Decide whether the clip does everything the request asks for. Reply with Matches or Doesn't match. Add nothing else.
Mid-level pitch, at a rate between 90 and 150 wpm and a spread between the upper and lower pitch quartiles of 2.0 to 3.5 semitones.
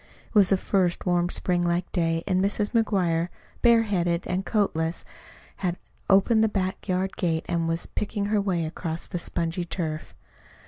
Doesn't match